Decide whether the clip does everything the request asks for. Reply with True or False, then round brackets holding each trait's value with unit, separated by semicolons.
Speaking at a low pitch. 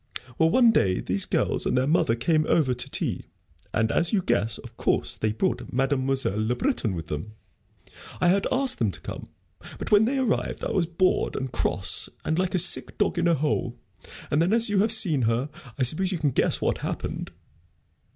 False (155 Hz)